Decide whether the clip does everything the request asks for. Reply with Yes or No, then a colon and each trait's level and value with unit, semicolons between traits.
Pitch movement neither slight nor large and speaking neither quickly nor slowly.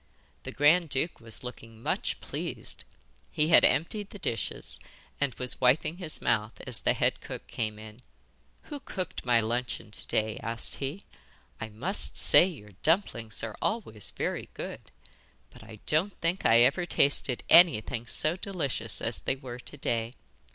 No: wide, 6.5 semitones; average, 160 wpm